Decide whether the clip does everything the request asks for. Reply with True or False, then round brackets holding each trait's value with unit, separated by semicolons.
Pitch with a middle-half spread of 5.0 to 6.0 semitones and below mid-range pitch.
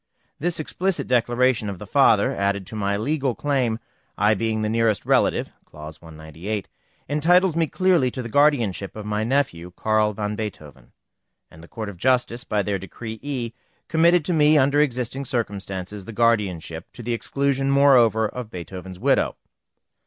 True (5.5 semitones; 115 Hz)